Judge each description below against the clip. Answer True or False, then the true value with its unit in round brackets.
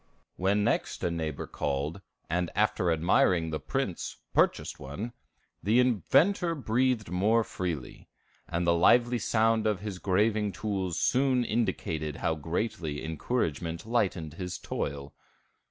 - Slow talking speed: True (125 wpm)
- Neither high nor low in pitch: False (95 Hz)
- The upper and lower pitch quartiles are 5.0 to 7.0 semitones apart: True (5.6 semitones)